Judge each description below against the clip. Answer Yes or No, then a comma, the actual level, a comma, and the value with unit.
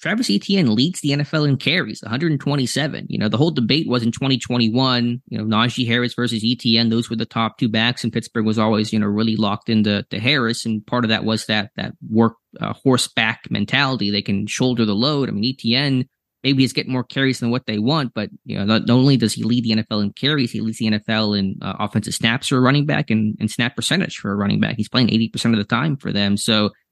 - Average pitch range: Yes, average, 3.1 semitones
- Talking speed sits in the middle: No, fast, 245 wpm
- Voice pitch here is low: Yes, low, 115 Hz